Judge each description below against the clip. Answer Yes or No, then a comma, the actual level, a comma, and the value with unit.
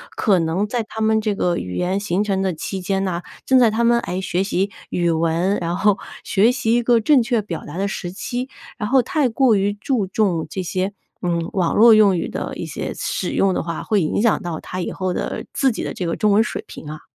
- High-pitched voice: Yes, high, 195 Hz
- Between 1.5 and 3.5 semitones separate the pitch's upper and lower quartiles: No, average, 4.0 semitones